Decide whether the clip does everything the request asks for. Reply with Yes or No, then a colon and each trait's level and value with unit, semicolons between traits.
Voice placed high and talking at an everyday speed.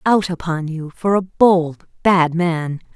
No: medium, 170 Hz; average, 160 wpm